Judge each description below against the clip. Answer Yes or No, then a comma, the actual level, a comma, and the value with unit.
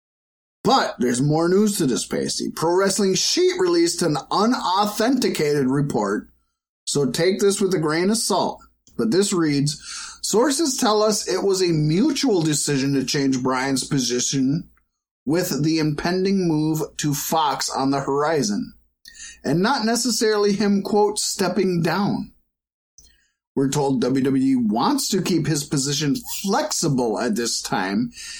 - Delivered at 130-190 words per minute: Yes, slow, 135 wpm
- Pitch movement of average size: No, wide, 7.0 semitones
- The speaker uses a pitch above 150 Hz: Yes, medium, 175 Hz